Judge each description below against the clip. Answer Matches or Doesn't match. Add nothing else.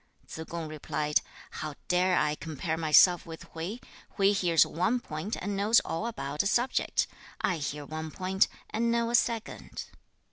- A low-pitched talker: Doesn't match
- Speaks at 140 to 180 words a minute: Matches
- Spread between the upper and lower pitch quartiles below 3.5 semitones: Doesn't match